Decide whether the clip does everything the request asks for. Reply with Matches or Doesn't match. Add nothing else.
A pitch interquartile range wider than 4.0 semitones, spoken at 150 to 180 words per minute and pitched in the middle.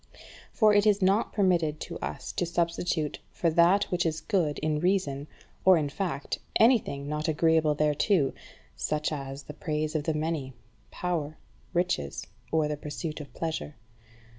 Doesn't match